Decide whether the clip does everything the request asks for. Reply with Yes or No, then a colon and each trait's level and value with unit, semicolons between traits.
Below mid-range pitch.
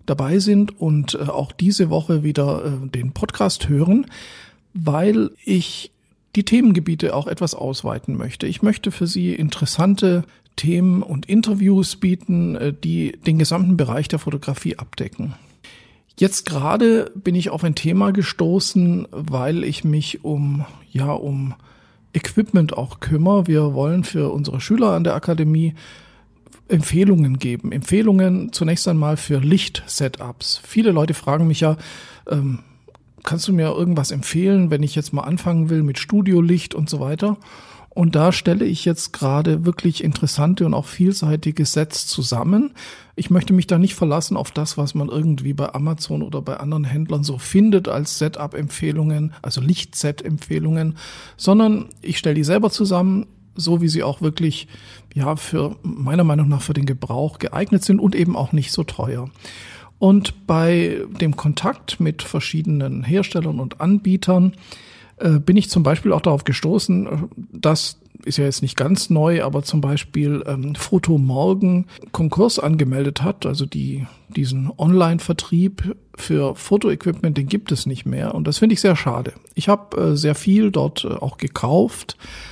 No: medium, 160 Hz